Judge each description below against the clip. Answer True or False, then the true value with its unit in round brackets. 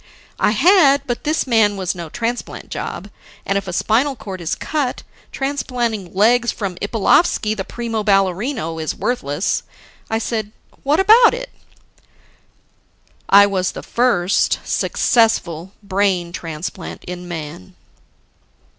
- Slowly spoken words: True (125 wpm)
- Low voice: False (210 Hz)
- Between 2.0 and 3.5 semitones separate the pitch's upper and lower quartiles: False (5.1 semitones)